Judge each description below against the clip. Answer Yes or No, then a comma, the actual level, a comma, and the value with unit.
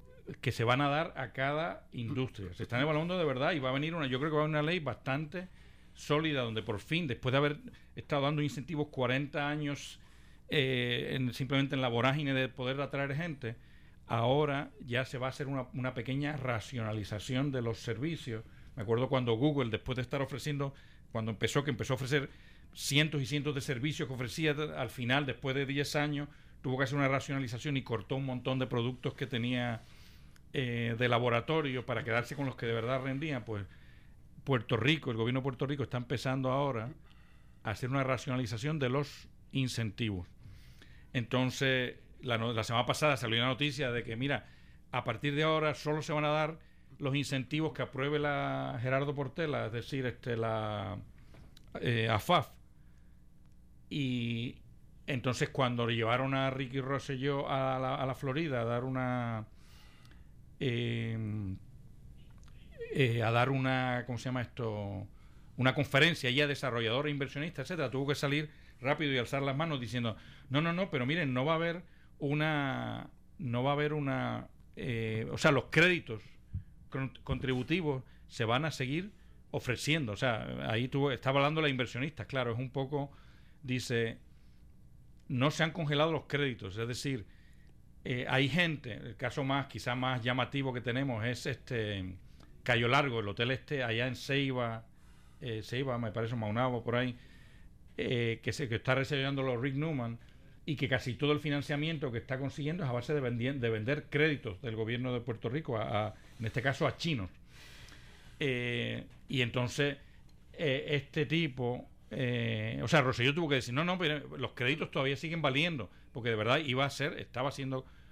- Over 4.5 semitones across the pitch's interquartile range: No, average, 3.4 semitones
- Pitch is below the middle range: Yes, low, 130 Hz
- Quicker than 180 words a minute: No, average, 175 wpm